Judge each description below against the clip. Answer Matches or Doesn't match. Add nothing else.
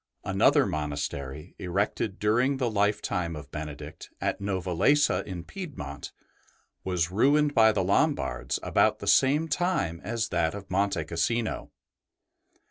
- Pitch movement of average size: Doesn't match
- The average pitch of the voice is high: Doesn't match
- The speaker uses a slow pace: Matches